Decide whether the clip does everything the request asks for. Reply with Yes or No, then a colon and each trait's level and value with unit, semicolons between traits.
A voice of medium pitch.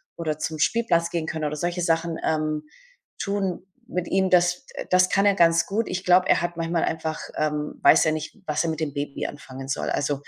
Yes: medium, 165 Hz